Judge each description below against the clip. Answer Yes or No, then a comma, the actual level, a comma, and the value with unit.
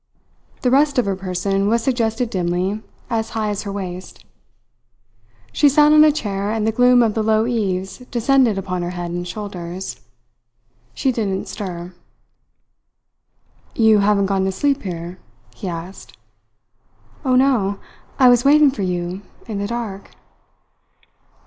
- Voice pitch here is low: No, high, 205 Hz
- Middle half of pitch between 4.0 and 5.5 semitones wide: Yes, average, 4.4 semitones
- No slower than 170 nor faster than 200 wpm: No, average, 145 wpm